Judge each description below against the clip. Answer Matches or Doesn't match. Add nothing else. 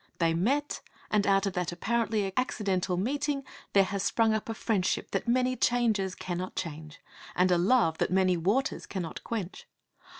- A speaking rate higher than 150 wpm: Matches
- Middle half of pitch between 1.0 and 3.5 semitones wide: Doesn't match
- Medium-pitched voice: Doesn't match